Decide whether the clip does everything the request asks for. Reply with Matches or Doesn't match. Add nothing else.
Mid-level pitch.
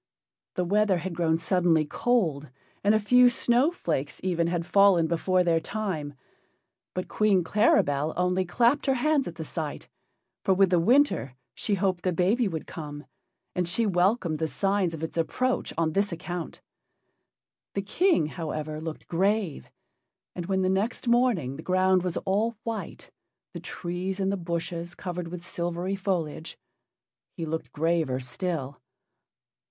Matches